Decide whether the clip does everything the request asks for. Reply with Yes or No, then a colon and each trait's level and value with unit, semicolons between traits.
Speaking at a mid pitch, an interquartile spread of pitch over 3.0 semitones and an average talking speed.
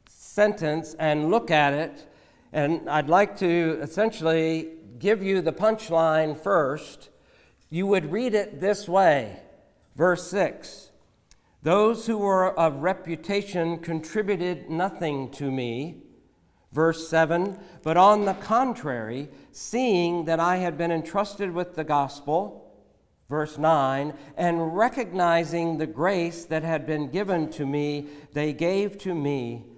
No: medium, 165 Hz; average, 3.8 semitones; slow, 125 wpm